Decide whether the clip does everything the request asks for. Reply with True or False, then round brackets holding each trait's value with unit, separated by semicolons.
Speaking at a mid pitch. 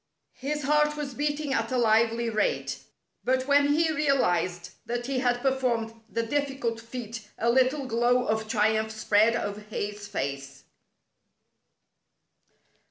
False (235 Hz)